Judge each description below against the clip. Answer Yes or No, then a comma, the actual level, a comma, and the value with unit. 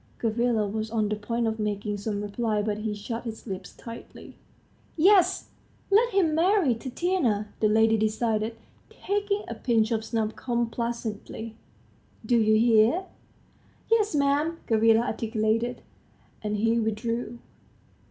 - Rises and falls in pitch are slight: Yes, narrow, 2.2 semitones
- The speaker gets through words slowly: Yes, slow, 130 wpm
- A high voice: Yes, high, 225 Hz